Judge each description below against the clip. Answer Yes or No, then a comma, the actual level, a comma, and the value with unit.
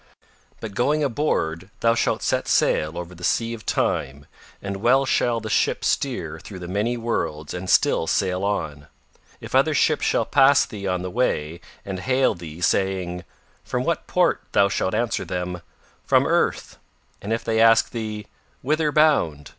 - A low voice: Yes, low, 100 Hz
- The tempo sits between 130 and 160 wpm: No, average, 170 wpm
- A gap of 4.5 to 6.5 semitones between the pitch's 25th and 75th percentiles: Yes, average, 4.9 semitones